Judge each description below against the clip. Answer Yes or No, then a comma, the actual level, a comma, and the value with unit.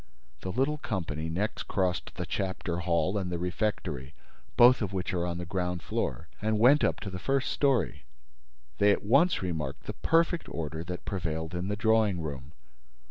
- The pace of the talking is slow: No, average, 180 wpm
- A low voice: Yes, very low, 90 Hz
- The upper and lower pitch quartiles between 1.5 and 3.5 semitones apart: No, average, 4.4 semitones